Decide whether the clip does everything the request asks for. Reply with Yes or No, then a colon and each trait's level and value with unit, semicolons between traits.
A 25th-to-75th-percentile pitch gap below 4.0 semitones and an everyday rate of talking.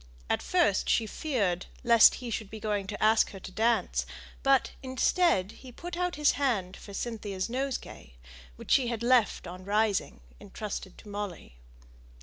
No: average, 4.6 semitones; average, 160 wpm